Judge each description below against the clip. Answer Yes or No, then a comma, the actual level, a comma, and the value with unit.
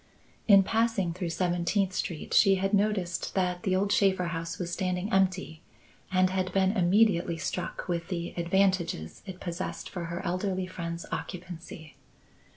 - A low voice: No, medium, 185 Hz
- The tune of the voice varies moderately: No, narrow, 2.0 semitones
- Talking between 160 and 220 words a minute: No, average, 150 wpm